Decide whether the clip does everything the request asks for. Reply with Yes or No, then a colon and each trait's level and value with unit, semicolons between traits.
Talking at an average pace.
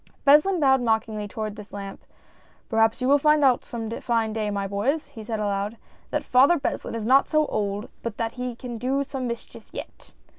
No: fast, 210 wpm